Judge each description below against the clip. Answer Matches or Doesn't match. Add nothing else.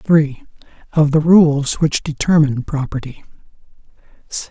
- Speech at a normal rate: Doesn't match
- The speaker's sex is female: Doesn't match